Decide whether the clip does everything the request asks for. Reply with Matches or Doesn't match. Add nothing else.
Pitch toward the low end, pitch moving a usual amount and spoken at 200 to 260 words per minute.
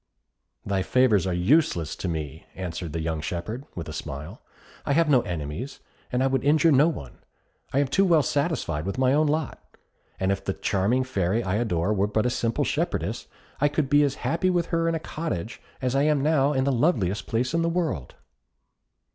Doesn't match